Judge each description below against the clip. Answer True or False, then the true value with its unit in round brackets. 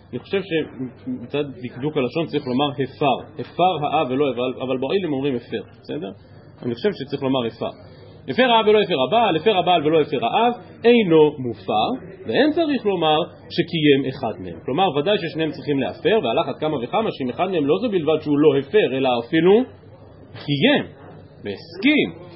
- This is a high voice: False (145 Hz)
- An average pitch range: False (5.7 semitones)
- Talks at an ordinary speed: False (165 wpm)